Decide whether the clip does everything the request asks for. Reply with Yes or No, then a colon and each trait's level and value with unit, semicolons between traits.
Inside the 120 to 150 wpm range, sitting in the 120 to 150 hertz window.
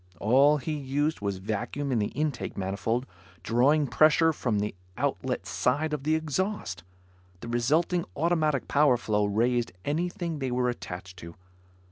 Yes: average, 145 wpm; low, 135 Hz